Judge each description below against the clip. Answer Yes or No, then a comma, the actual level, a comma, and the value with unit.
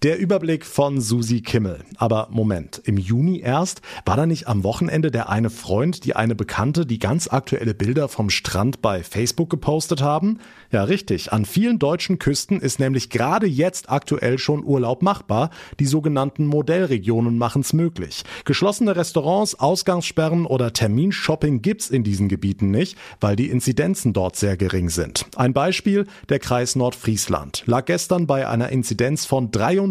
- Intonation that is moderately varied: No, wide, 6.5 semitones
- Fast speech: No, average, 160 wpm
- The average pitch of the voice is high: No, low, 135 Hz